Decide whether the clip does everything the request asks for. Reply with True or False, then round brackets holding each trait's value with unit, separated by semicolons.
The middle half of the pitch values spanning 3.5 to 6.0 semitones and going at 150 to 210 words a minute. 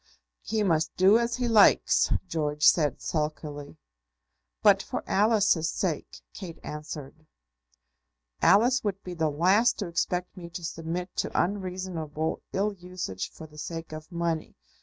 False (3.9 semitones; 140 wpm)